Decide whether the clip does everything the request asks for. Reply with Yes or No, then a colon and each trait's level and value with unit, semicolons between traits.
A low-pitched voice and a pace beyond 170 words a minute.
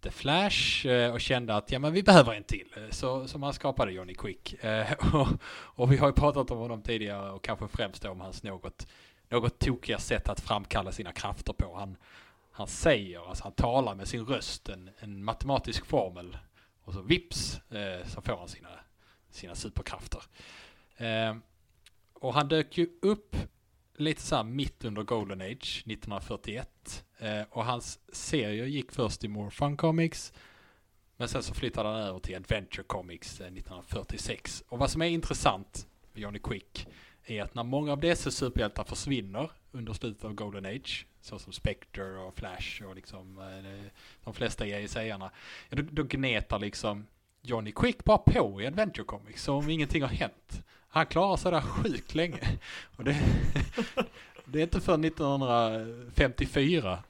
No: low, 110 Hz; average, 160 wpm